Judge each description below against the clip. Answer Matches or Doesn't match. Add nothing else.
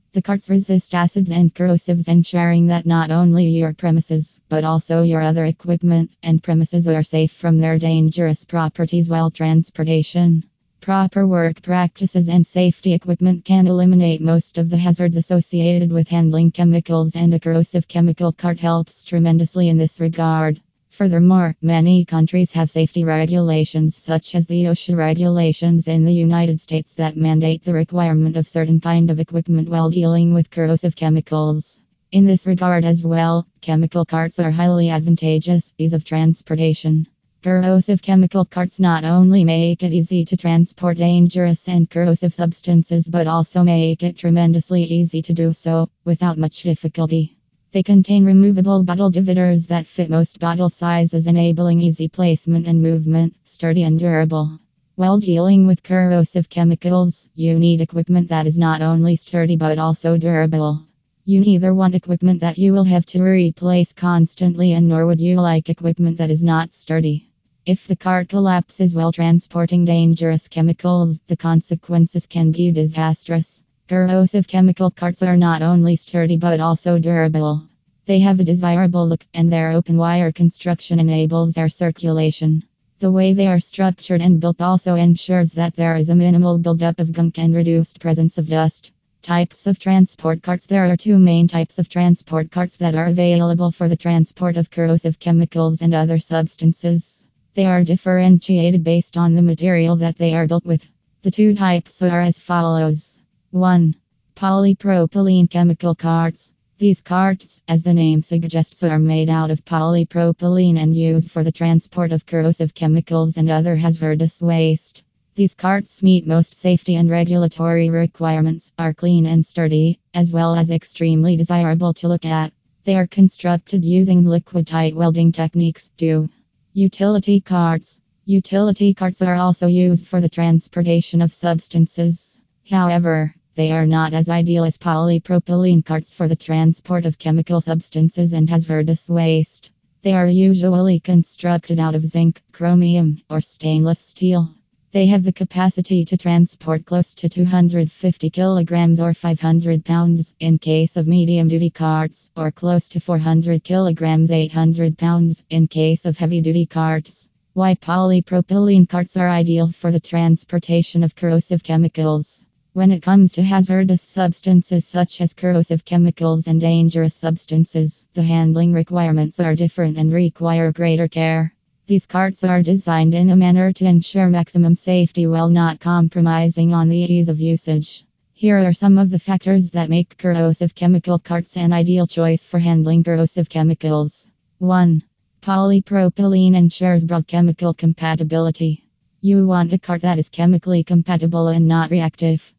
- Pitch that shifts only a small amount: Matches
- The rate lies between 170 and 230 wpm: Doesn't match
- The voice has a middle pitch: Matches